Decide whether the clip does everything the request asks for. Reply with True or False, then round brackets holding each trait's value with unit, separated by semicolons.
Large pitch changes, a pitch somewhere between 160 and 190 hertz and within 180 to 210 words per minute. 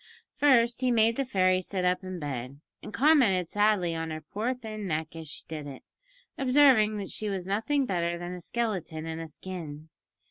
True (5.8 semitones; 185 Hz; 190 wpm)